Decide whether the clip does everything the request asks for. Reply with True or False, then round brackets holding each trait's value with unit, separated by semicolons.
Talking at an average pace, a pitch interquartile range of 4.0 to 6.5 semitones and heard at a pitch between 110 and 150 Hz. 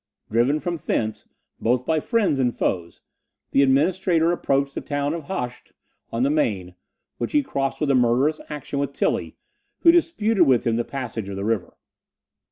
True (175 wpm; 5.3 semitones; 140 Hz)